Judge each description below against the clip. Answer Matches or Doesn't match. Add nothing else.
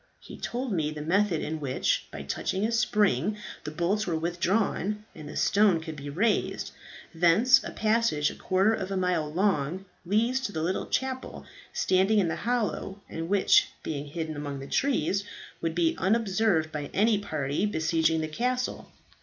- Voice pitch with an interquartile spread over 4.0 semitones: Matches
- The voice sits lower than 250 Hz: Matches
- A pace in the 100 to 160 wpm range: Doesn't match